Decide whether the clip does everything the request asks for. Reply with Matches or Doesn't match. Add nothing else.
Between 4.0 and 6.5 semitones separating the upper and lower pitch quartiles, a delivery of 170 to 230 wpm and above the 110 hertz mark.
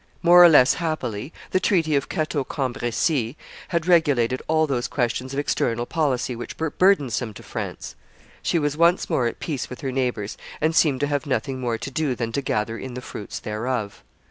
Matches